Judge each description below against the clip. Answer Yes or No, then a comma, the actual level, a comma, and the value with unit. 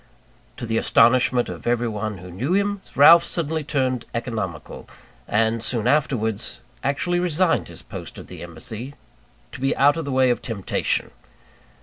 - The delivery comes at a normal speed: Yes, average, 150 wpm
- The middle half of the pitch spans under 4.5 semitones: No, average, 4.9 semitones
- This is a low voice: Yes, low, 125 Hz